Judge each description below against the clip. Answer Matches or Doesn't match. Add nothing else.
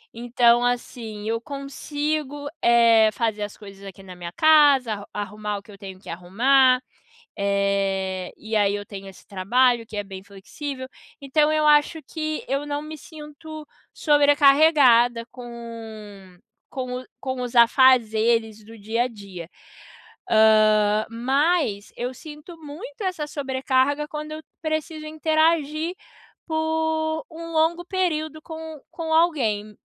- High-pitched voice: Matches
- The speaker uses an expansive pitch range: Matches